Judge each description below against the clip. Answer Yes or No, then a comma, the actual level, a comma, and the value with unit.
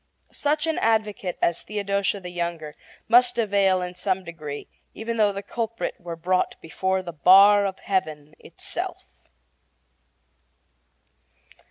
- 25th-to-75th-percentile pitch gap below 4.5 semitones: Yes, average, 3.4 semitones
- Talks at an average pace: No, slow, 125 wpm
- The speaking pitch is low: No, high, 190 Hz